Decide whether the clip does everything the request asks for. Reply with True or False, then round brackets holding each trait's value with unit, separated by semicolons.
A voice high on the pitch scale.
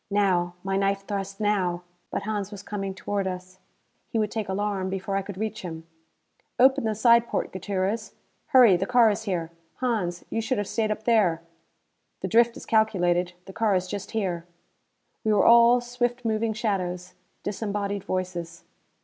True (200 Hz)